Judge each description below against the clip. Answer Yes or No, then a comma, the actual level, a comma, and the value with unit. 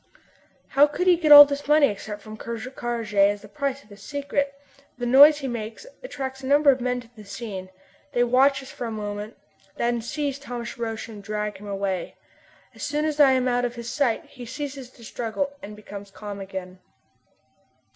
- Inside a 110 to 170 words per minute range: No, fast, 205 wpm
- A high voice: Yes, high, 240 Hz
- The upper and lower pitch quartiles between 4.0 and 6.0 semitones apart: Yes, average, 4.8 semitones